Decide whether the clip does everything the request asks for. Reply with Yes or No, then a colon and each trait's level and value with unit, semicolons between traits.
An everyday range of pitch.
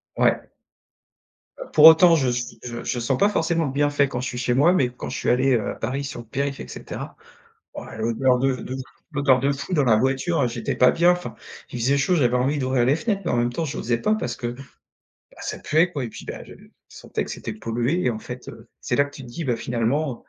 Yes: average, 3.2 semitones